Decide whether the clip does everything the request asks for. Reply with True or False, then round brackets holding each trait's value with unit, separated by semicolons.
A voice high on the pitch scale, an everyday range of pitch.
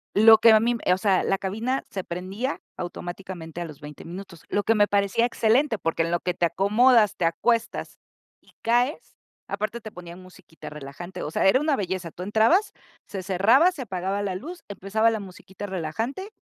True (200 Hz; 4.2 semitones)